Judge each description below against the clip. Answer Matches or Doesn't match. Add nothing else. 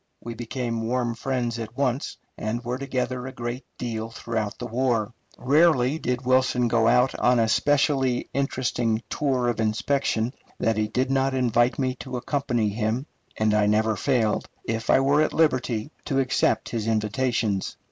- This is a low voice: Matches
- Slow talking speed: Doesn't match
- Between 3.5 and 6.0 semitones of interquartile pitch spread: Doesn't match